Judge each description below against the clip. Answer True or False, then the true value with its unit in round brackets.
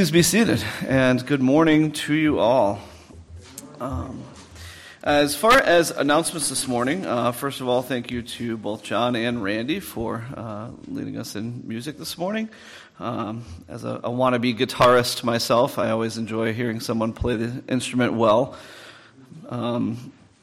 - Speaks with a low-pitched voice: True (120 Hz)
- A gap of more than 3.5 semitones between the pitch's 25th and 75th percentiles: True (4.0 semitones)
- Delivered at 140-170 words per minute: True (155 wpm)